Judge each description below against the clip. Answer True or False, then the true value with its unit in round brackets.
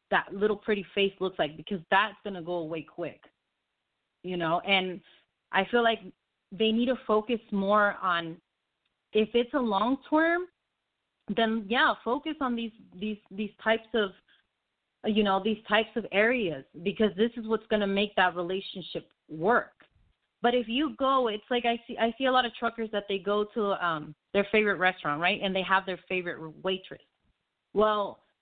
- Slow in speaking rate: False (180 wpm)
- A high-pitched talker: True (210 Hz)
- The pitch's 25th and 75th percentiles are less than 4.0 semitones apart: True (3.6 semitones)